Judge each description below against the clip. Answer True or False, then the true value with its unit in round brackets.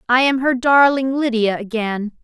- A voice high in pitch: True (245 Hz)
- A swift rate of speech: False (160 wpm)